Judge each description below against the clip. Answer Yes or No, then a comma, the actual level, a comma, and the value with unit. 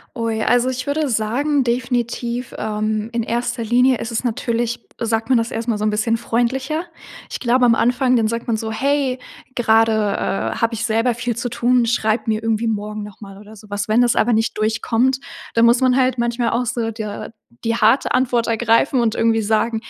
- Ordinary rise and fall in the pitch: No, narrow, 1.9 semitones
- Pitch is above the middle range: Yes, high, 230 Hz